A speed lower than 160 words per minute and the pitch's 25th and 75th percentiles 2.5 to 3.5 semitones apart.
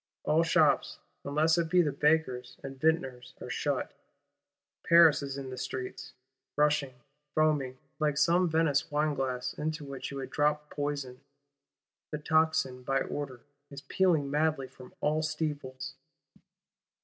Yes: slow, 135 wpm; average, 2.9 semitones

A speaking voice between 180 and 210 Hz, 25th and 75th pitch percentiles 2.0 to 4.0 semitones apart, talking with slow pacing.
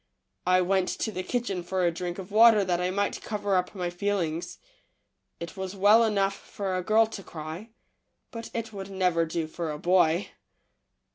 No: high, 190 Hz; narrow, 2.6 semitones; average, 185 wpm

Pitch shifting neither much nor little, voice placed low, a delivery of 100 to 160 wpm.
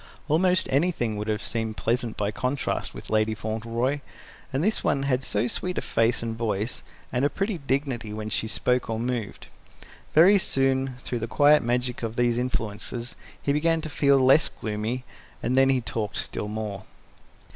No: average, 3.8 semitones; low, 125 Hz; average, 175 wpm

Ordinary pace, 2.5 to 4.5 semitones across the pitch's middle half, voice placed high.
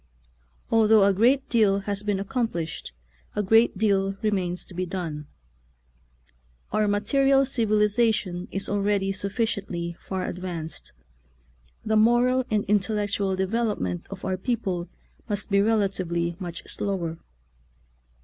No: slow, 120 wpm; average, 2.8 semitones; high, 200 Hz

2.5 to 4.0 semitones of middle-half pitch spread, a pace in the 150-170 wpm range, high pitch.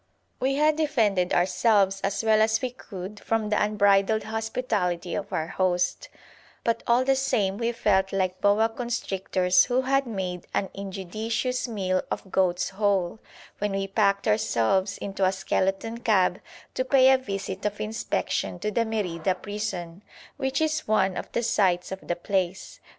Yes: average, 3.1 semitones; average, 160 wpm; high, 205 Hz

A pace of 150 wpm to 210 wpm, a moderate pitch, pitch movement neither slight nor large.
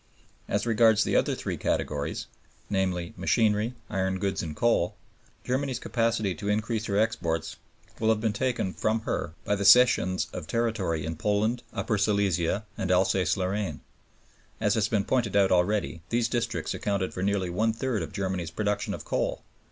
No: average, 165 wpm; low, 100 Hz; average, 3.3 semitones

